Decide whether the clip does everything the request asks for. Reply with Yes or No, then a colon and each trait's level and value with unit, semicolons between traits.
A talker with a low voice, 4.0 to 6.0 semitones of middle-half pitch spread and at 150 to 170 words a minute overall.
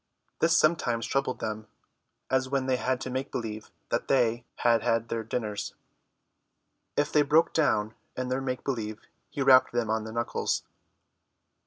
No: low, 125 Hz; average, 3.0 semitones; average, 160 wpm